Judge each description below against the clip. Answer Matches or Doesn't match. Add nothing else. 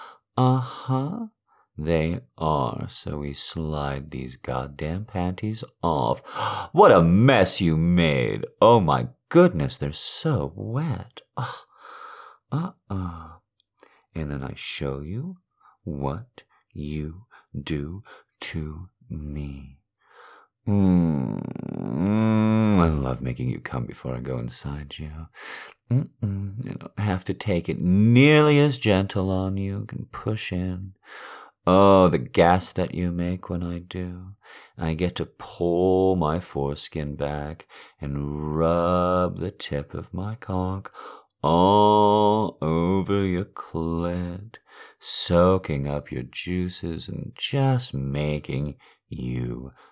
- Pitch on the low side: Matches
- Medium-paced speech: Doesn't match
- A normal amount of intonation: Doesn't match